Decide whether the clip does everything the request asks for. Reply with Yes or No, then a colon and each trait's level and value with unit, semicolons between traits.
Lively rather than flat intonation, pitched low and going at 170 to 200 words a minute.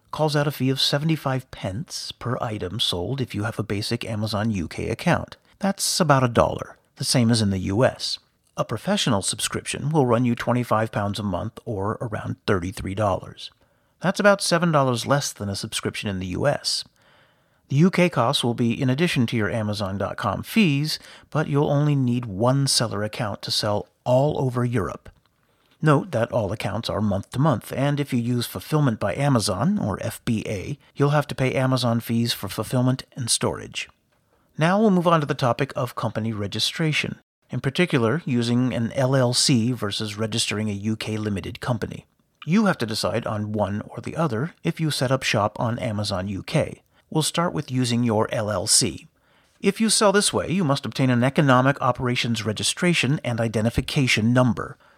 No: average, 4.7 semitones; low, 125 Hz; average, 175 wpm